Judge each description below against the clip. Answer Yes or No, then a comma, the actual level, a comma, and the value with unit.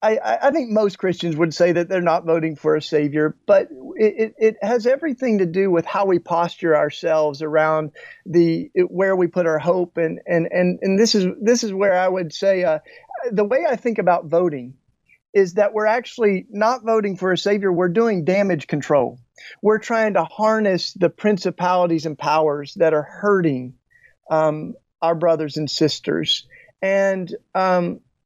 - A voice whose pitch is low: No, medium, 180 Hz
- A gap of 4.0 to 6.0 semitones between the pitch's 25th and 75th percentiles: Yes, average, 4.4 semitones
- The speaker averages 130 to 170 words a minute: No, average, 180 wpm